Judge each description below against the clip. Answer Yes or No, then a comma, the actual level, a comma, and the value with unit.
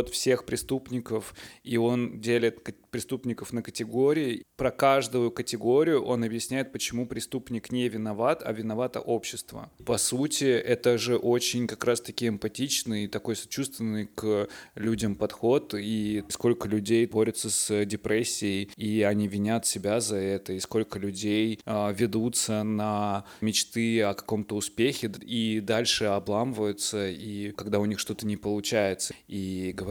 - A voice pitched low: Yes, low, 110 Hz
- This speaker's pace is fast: No, average, 135 wpm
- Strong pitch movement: No, narrow, 2.4 semitones